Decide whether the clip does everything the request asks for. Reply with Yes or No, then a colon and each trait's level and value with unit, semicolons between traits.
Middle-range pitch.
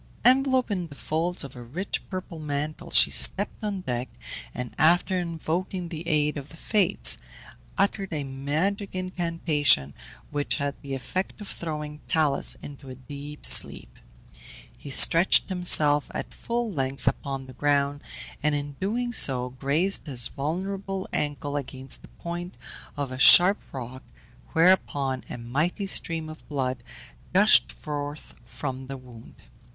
Yes: medium, 150 Hz